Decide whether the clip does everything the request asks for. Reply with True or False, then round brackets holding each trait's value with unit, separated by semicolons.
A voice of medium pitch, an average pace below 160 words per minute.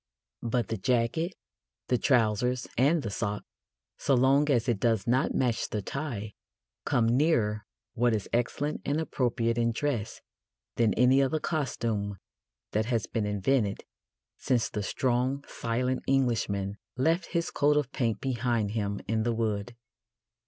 False (120 Hz; 145 wpm)